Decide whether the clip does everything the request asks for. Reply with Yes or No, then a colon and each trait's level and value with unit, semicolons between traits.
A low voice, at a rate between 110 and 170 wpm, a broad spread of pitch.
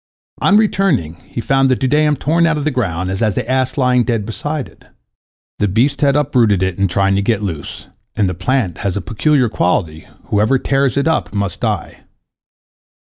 No: low, 120 Hz; average, 185 wpm; wide, 6.1 semitones